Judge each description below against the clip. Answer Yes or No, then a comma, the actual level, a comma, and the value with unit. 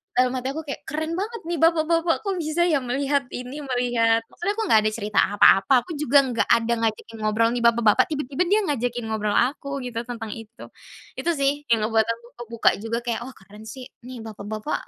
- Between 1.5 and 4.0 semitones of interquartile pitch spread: No, average, 4.5 semitones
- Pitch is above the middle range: Yes, high, 245 Hz